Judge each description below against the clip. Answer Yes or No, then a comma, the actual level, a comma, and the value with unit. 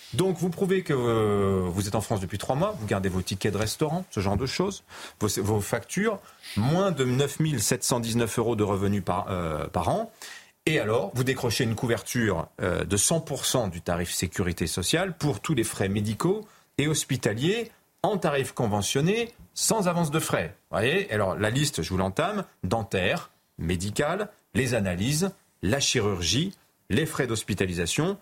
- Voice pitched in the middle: No, low, 120 Hz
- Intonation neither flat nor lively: No, wide, 7.6 semitones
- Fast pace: No, average, 165 wpm